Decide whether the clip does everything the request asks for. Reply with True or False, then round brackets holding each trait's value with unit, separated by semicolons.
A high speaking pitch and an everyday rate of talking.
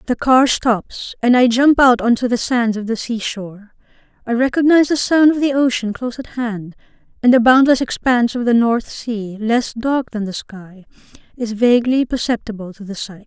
True (235 Hz; 195 wpm)